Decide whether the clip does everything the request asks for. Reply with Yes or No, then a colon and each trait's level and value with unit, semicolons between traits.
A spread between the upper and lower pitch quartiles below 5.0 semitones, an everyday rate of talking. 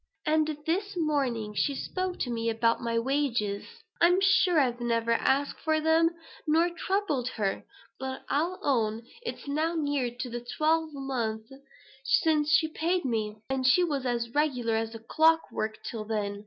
No: wide, 5.5 semitones; average, 160 wpm